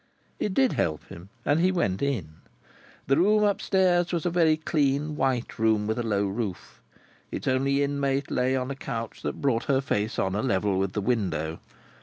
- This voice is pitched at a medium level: No, low, 130 Hz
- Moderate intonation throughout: No, wide, 6.5 semitones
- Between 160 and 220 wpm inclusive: Yes, average, 195 wpm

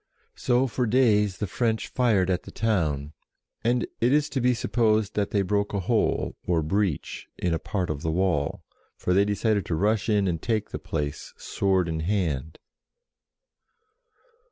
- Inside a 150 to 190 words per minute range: Yes, average, 170 wpm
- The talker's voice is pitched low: Yes, low, 100 Hz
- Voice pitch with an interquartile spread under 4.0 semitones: No, average, 4.5 semitones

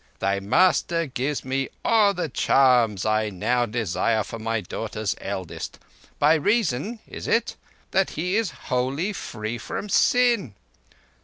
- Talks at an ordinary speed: No, slow, 125 wpm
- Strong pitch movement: Yes, wide, 8.8 semitones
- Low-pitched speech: Yes, low, 130 Hz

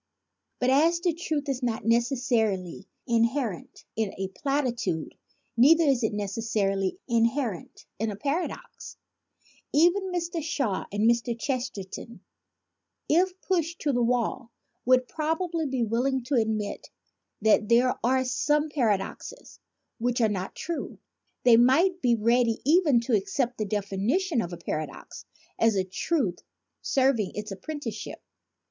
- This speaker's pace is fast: No, slow, 135 wpm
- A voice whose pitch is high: Yes, high, 245 Hz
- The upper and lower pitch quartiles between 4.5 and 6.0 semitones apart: Yes, average, 5.2 semitones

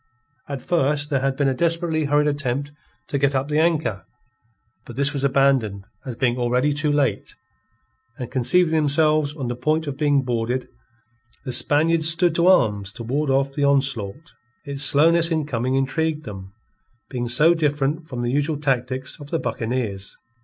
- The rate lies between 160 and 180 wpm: Yes, average, 170 wpm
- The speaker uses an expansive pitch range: No, average, 3.3 semitones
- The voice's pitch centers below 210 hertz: Yes, medium, 140 Hz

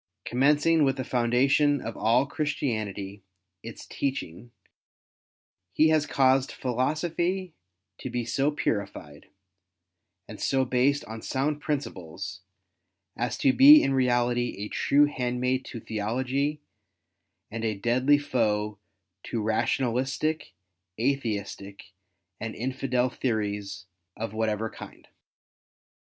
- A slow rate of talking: Yes, slow, 105 wpm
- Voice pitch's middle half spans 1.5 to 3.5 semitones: No, average, 4.0 semitones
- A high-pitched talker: No, low, 125 Hz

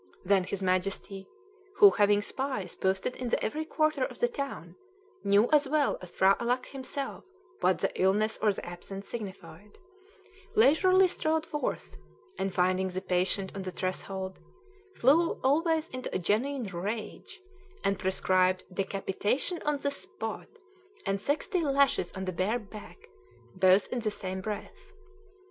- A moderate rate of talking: Yes, average, 145 wpm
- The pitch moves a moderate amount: No, wide, 6.8 semitones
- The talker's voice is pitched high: Yes, high, 205 Hz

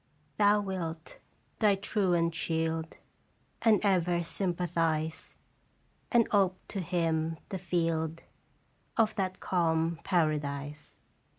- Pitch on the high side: No, medium, 170 Hz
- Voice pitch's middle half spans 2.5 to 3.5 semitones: Yes, average, 3.0 semitones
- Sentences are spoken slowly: Yes, slow, 100 wpm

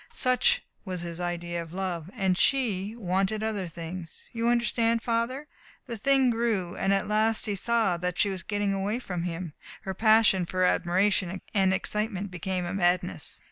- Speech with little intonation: No, average, 3.9 semitones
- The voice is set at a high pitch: Yes, high, 195 Hz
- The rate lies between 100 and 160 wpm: No, average, 170 wpm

